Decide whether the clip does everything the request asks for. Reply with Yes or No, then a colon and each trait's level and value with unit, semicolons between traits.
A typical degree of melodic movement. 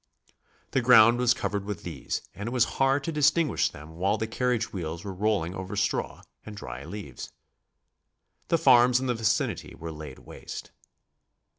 No: wide, 6.0 semitones